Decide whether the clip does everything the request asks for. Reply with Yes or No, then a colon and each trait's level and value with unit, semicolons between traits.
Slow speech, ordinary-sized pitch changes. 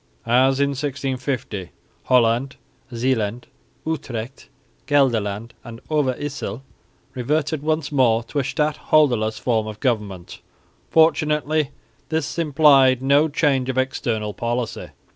Yes: slow, 105 wpm; average, 4.0 semitones